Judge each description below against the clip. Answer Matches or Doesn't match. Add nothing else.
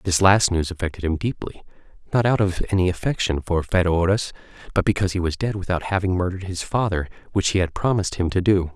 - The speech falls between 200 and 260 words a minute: Matches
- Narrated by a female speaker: Doesn't match